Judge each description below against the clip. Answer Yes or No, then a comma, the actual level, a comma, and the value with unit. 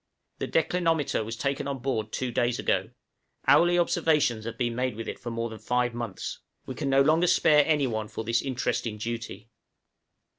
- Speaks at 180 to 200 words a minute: Yes, average, 185 wpm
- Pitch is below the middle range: Yes, low, 125 Hz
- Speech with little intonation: No, average, 3.8 semitones